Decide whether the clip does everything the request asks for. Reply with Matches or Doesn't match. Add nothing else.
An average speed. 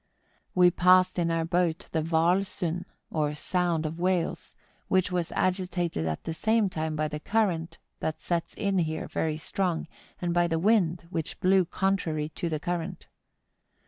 Matches